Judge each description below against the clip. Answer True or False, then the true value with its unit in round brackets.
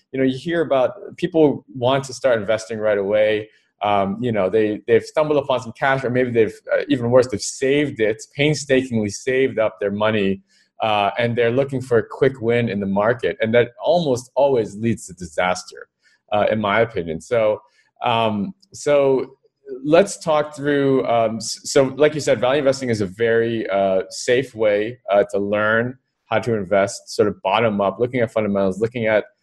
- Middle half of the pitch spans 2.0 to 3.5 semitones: False (4.8 semitones)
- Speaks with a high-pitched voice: False (120 Hz)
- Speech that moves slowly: False (185 wpm)